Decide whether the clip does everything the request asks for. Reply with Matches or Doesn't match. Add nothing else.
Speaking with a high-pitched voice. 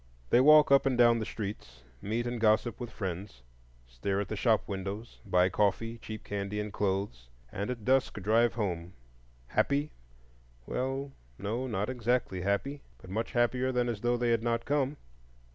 Doesn't match